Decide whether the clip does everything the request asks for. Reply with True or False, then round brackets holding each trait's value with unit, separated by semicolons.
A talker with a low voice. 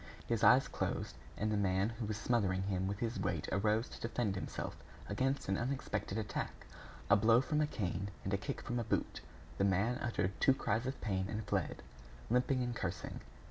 True (105 Hz)